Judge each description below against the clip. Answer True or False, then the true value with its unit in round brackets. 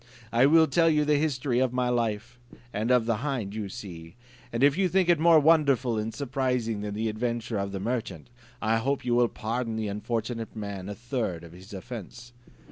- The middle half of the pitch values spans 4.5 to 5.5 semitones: False (3.9 semitones)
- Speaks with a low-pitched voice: True (120 Hz)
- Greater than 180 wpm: True (205 wpm)